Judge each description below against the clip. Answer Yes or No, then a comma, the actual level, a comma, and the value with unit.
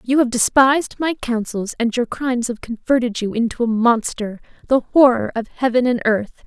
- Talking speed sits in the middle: Yes, average, 185 wpm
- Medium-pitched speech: No, high, 240 Hz